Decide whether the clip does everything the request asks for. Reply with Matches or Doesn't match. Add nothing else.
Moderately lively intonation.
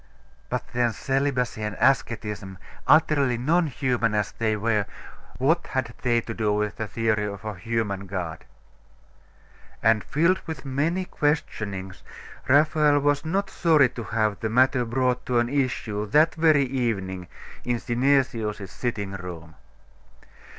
Matches